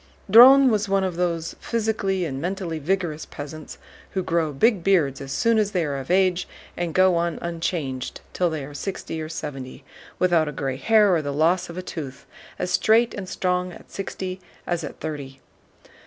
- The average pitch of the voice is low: No, medium, 175 Hz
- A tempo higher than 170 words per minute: Yes, average, 185 wpm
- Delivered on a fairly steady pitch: No, average, 3.9 semitones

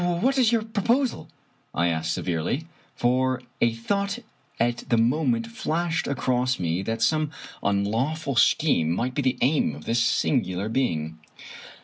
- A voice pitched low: Yes, low, 125 Hz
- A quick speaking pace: No, average, 145 wpm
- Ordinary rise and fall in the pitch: No, wide, 7.7 semitones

